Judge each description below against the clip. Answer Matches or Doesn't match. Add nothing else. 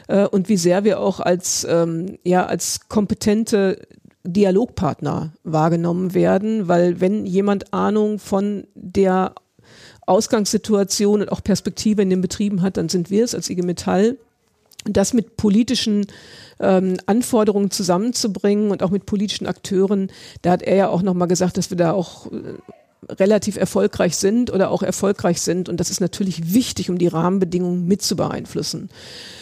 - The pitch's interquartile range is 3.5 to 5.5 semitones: Doesn't match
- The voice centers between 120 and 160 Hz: Doesn't match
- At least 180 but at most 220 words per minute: Doesn't match